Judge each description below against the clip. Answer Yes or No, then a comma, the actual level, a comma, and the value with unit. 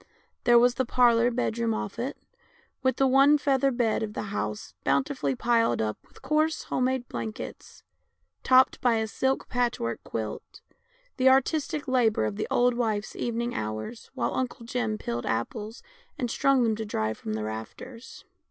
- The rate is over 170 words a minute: No, average, 165 wpm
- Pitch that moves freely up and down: No, average, 3.7 semitones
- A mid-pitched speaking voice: No, high, 235 Hz